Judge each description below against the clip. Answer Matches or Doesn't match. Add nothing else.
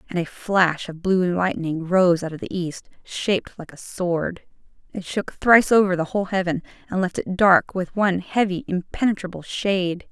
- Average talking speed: Matches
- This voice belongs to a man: Doesn't match